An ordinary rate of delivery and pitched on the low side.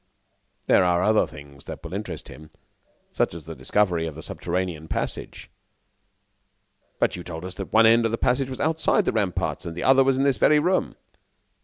Yes: average, 195 wpm; very low, 95 Hz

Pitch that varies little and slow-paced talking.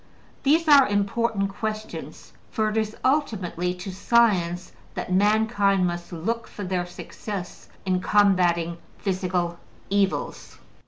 No: average, 3.3 semitones; slow, 115 wpm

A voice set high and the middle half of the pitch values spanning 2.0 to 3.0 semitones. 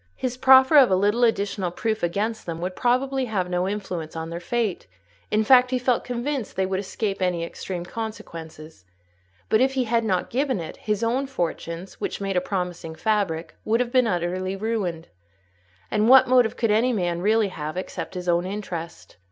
No: high, 205 Hz; average, 5.0 semitones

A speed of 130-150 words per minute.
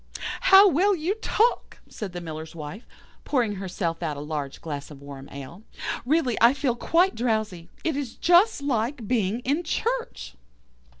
No: average, 160 wpm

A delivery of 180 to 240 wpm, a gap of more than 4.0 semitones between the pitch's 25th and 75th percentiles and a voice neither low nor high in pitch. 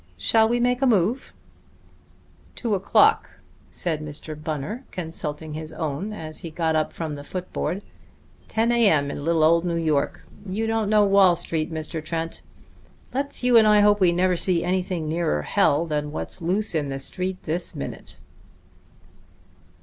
No: average, 165 wpm; average, 4.9 semitones; medium, 170 Hz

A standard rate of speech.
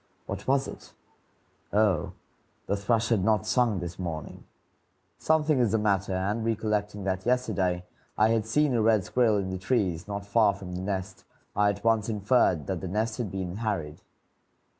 Yes: average, 175 wpm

